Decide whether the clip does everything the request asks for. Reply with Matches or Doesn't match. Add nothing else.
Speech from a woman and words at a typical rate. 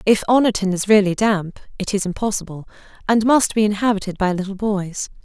Matches